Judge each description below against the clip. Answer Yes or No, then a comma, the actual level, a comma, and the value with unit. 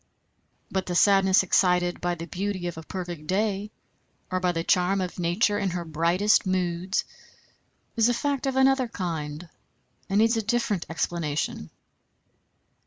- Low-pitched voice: No, medium, 185 Hz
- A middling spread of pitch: Yes, average, 3.2 semitones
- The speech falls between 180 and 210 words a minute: No, average, 150 wpm